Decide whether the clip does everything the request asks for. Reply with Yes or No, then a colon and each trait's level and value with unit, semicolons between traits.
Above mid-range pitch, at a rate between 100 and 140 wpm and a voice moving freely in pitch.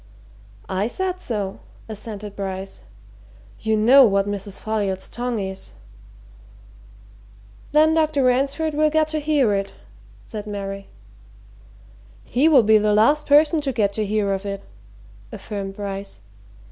Yes: high, 215 Hz; slow, 135 wpm; wide, 6.4 semitones